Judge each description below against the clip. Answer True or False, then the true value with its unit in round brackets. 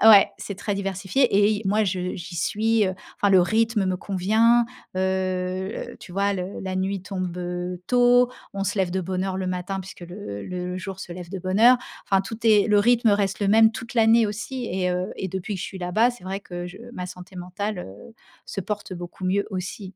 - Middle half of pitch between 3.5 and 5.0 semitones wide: False (2.6 semitones)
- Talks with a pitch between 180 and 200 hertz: True (190 Hz)